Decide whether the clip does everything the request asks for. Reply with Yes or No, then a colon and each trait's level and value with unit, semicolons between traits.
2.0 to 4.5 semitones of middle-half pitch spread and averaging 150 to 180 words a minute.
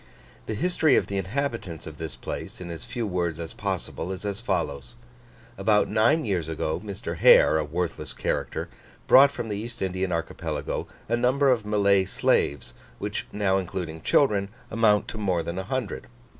No: average, 5.0 semitones; average, 170 wpm